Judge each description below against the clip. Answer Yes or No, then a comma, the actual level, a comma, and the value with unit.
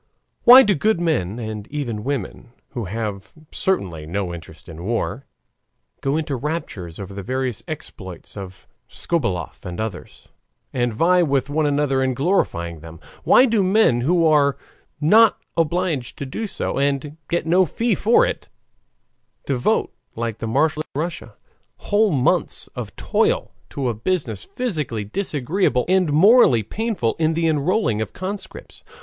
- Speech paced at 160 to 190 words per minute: No, average, 150 wpm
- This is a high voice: No, medium, 140 Hz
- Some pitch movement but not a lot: No, wide, 7.8 semitones